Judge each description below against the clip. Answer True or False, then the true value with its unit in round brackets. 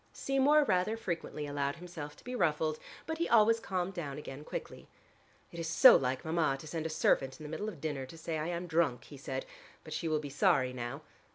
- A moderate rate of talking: False (220 wpm)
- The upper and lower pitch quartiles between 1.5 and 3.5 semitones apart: False (4.1 semitones)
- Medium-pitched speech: True (160 Hz)